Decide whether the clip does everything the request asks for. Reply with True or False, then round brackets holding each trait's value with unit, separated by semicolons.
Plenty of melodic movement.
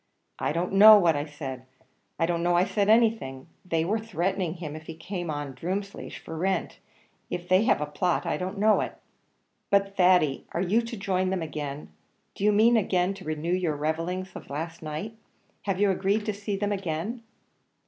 False (3.9 semitones)